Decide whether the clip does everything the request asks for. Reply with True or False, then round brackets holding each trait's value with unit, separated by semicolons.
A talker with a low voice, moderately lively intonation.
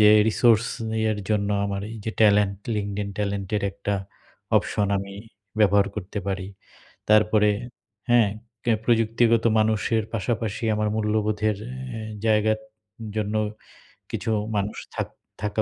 False (105 Hz; 1.4 semitones)